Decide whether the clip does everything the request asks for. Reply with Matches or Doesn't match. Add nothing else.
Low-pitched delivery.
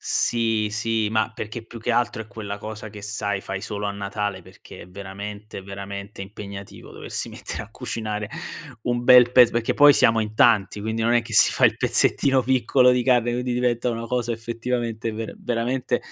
Matches